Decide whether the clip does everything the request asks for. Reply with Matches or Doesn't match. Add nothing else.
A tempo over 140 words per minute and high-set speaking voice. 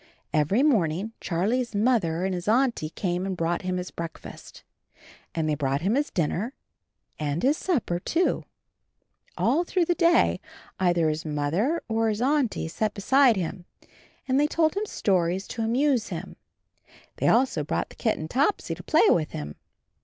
Matches